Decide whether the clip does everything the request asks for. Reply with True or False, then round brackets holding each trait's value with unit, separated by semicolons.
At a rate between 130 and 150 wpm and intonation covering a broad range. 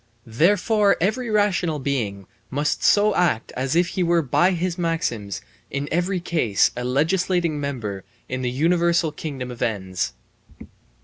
True (140 wpm; 6.1 semitones)